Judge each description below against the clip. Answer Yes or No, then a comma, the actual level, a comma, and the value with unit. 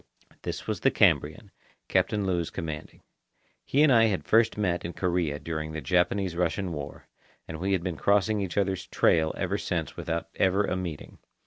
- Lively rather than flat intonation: No, average, 3.3 semitones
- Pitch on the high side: No, very low, 90 Hz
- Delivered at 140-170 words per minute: No, average, 180 wpm